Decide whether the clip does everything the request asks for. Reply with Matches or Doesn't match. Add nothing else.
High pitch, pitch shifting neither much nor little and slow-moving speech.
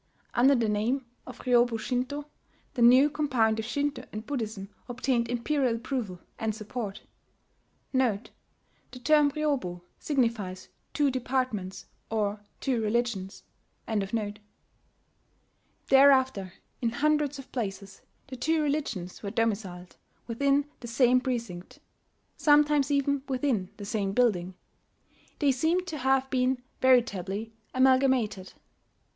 Matches